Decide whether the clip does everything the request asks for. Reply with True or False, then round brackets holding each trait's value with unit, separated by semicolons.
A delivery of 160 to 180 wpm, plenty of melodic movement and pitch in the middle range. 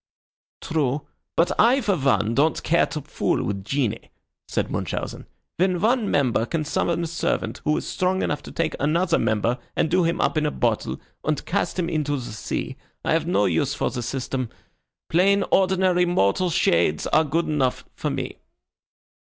True (175 wpm; 6.1 semitones; 155 Hz)